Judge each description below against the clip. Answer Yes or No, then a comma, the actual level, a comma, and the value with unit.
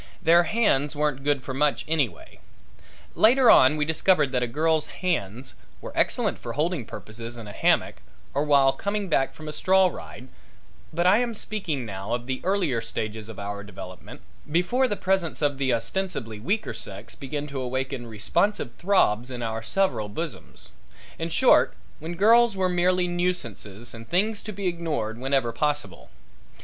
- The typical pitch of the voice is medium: Yes, medium, 145 Hz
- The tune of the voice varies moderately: No, wide, 7.5 semitones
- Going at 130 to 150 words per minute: No, average, 165 wpm